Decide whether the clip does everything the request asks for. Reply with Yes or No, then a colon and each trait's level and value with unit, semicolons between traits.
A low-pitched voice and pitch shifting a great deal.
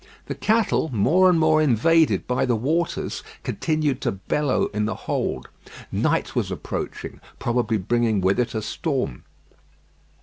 Yes: low, 125 Hz; wide, 6.3 semitones